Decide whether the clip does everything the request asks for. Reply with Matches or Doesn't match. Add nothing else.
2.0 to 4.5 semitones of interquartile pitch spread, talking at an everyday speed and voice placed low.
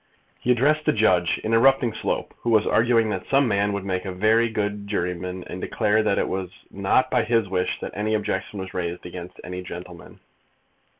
Matches